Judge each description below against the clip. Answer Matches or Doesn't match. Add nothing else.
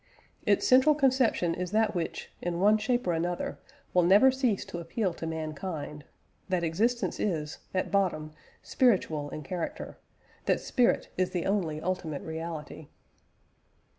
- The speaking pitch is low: Doesn't match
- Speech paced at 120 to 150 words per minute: Matches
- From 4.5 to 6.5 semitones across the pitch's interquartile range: Matches